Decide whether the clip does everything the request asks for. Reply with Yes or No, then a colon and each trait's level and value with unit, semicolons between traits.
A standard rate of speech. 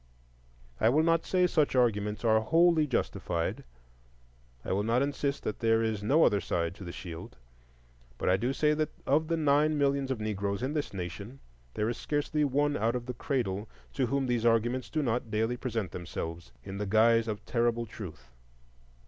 Yes: average, 180 wpm